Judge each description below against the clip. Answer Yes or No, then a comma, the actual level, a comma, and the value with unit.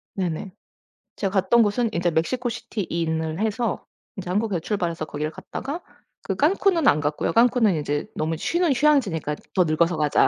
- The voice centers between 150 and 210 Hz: Yes, high, 190 Hz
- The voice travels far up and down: Yes, wide, 6.8 semitones